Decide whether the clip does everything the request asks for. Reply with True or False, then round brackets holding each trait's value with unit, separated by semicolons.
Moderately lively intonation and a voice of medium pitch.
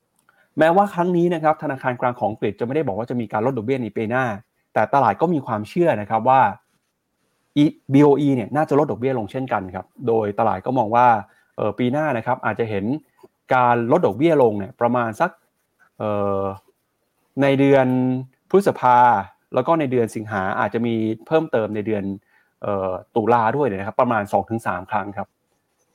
False (4.1 semitones; 125 Hz)